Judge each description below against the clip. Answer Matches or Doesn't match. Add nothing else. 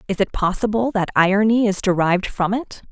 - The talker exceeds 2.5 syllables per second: Matches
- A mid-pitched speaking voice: Doesn't match